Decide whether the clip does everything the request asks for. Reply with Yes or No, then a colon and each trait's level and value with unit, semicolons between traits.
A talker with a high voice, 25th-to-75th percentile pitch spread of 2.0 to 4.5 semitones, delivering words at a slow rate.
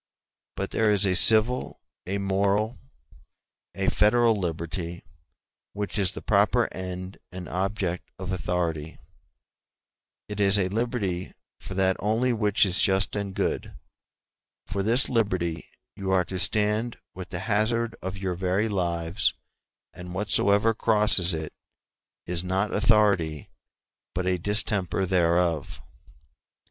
No: very low, 95 Hz; average, 2.9 semitones; slow, 125 wpm